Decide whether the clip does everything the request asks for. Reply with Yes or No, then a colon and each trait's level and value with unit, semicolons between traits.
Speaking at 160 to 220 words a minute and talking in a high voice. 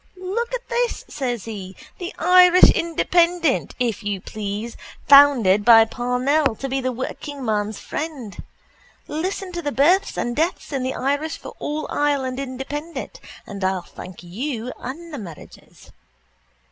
No: average, 140 wpm; very high, 270 Hz